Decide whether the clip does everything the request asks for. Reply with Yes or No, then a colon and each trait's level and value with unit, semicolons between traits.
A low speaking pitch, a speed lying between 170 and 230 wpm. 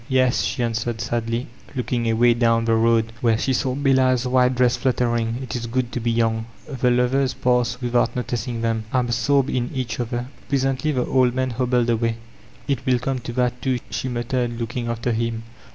Yes: low, 120 Hz; average, 185 wpm